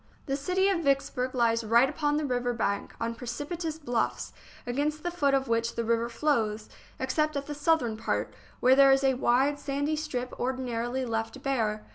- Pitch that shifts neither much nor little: Yes, average, 3.8 semitones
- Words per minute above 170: Yes, average, 180 wpm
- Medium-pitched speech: No, very high, 260 Hz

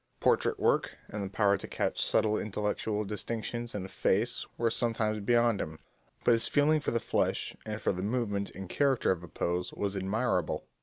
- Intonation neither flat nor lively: Yes, average, 3.0 semitones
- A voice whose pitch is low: Yes, low, 105 Hz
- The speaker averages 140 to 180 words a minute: No, average, 190 wpm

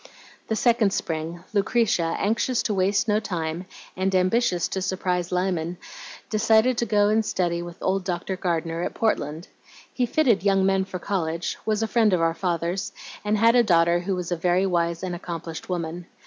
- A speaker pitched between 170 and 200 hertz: Yes, medium, 185 Hz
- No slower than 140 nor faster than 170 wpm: No, average, 180 wpm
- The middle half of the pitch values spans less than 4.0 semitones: Yes, average, 3.5 semitones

